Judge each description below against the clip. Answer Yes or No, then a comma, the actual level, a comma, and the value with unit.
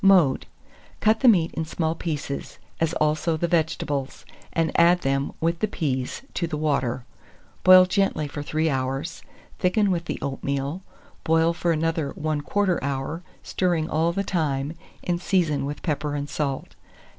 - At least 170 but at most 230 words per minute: No, average, 155 wpm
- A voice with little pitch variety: No, average, 3.2 semitones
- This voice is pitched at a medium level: Yes, medium, 160 Hz